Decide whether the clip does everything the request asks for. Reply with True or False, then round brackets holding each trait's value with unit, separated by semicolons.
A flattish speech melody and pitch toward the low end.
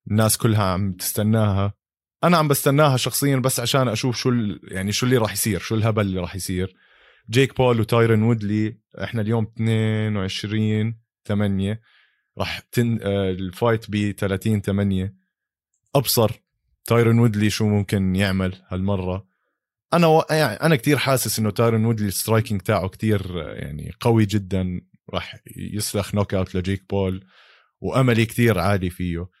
False (3.1 semitones; 105 Hz)